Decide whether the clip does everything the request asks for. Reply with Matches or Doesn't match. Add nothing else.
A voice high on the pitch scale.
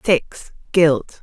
Doesn't match